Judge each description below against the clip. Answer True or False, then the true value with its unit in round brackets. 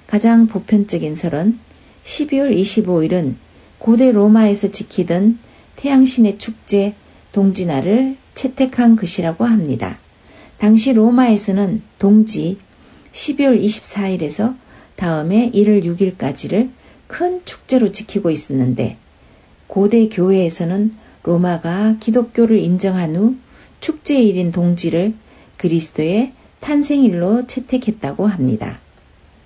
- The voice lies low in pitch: False (205 Hz)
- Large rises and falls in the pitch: False (4.8 semitones)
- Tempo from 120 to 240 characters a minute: True (230 characters per minute)